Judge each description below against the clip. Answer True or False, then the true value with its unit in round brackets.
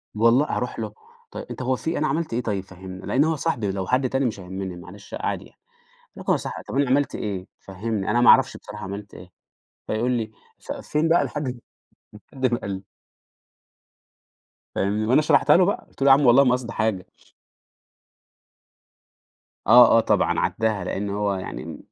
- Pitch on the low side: True (115 Hz)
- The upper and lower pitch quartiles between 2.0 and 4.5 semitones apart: False (5.2 semitones)